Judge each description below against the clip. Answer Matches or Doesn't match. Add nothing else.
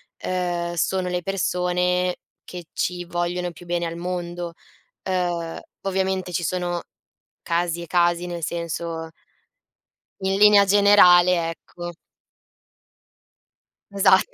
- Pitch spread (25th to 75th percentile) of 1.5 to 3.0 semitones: Doesn't match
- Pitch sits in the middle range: Matches